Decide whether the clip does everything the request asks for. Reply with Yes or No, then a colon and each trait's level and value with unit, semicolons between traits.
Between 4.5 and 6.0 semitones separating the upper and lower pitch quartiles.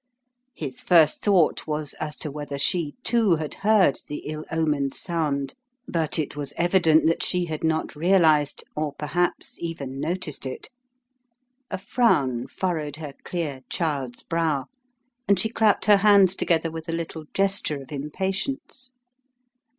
No: average, 3.8 semitones